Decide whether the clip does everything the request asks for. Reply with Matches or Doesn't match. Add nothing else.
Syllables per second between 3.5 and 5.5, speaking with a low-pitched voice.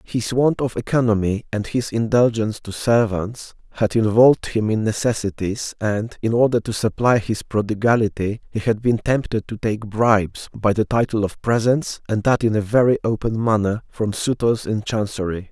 Matches